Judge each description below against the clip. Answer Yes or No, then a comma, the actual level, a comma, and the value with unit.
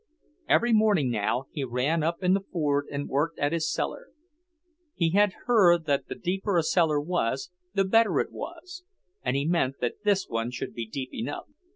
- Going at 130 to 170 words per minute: No, average, 190 wpm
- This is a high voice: No, medium, 165 Hz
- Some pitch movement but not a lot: No, wide, 5.8 semitones